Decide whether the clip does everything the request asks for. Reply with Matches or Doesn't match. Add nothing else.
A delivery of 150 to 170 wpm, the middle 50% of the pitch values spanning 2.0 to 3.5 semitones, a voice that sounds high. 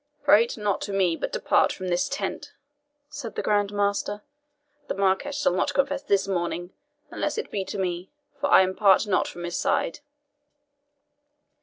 Matches